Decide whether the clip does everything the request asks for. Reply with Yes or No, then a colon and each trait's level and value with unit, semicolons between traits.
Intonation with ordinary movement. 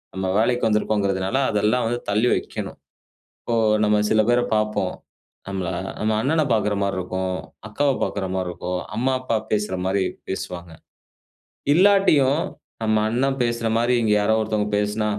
Yes: average, 3.7 semitones